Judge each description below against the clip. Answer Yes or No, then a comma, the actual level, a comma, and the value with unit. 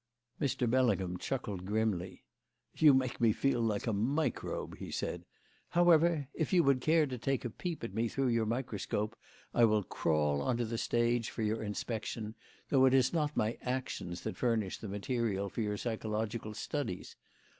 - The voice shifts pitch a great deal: No, average, 3.7 semitones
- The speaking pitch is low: Yes, low, 115 Hz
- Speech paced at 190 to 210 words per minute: No, average, 175 wpm